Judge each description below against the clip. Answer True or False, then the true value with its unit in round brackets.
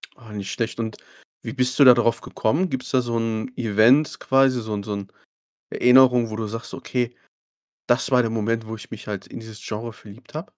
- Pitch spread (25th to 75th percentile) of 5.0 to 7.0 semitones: False (2.4 semitones)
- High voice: False (115 Hz)